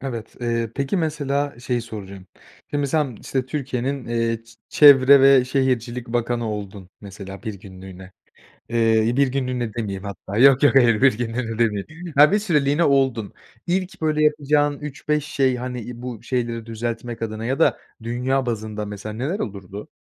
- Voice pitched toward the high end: No, low, 120 Hz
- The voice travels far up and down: No, average, 3.8 semitones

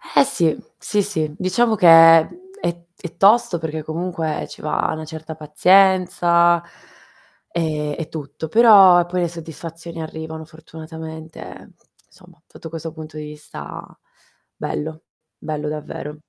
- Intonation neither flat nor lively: No, narrow, 1.9 semitones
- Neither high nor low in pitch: Yes, medium, 165 Hz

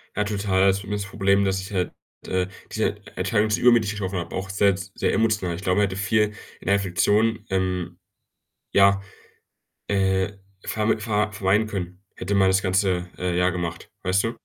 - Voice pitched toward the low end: Yes, very low, 95 Hz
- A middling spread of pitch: No, narrow, 1.8 semitones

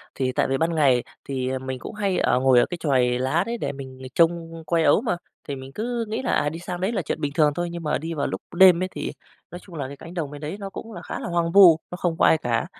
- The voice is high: No, medium, 165 Hz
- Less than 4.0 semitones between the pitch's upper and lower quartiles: No, average, 4.5 semitones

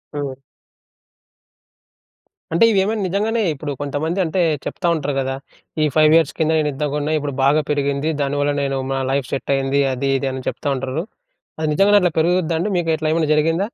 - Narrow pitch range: No, average, 3.0 semitones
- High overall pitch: No, medium, 150 Hz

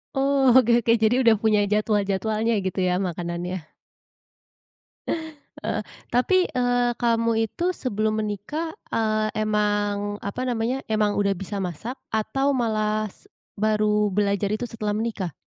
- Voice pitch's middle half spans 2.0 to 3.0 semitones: Yes, narrow, 2.5 semitones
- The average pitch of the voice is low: No, high, 215 Hz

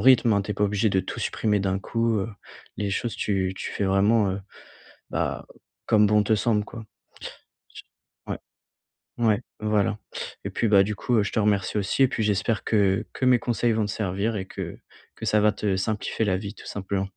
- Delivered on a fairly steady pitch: Yes, narrow, 2.0 semitones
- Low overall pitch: Yes, low, 105 Hz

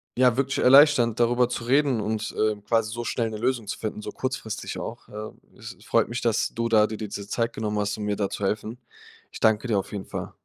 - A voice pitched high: No, low, 115 Hz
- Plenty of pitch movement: No, narrow, 2.4 semitones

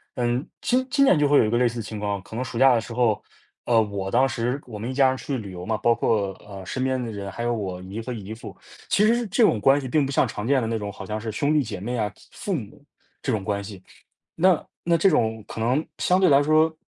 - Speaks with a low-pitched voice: Yes, low, 120 Hz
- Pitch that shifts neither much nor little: Yes, average, 4.7 semitones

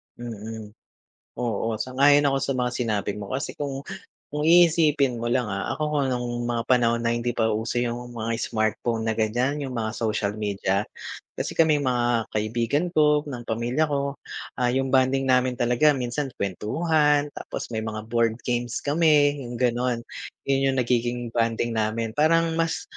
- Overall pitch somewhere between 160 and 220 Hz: No, low, 120 Hz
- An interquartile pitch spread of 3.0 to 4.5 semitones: Yes, average, 3.5 semitones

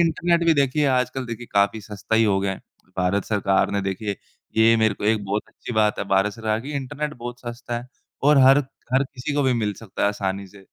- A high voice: No, low, 110 Hz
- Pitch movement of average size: Yes, average, 4.5 semitones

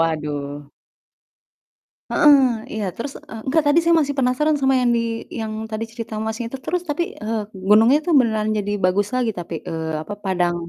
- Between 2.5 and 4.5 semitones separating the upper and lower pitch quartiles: No, wide, 5.5 semitones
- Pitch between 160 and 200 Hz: No, high, 225 Hz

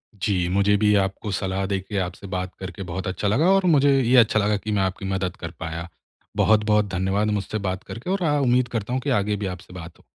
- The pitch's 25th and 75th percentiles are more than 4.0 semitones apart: No, narrow, 2.6 semitones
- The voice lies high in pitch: No, low, 100 Hz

